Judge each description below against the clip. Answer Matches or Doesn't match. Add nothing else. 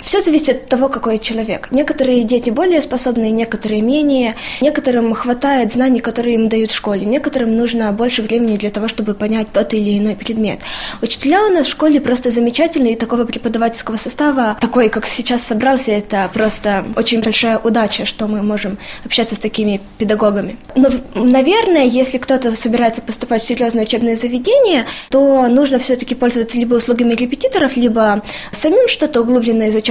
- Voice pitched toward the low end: Doesn't match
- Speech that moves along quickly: Matches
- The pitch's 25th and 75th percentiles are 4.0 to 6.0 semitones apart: Doesn't match